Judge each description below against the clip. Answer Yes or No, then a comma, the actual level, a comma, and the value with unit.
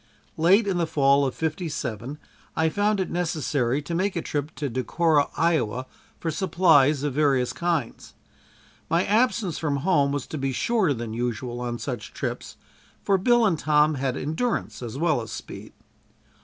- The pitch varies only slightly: No, average, 4.6 semitones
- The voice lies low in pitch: No, medium, 150 Hz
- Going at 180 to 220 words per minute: No, average, 165 wpm